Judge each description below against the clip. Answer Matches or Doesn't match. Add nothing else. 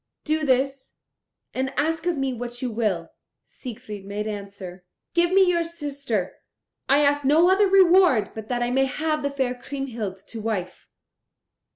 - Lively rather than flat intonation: Matches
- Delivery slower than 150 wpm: Doesn't match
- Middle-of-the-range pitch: Doesn't match